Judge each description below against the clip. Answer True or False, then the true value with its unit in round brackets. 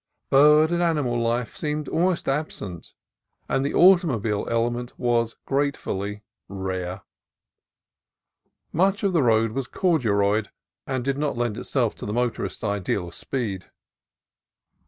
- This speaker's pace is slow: True (125 wpm)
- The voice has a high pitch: False (120 Hz)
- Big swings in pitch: True (6.3 semitones)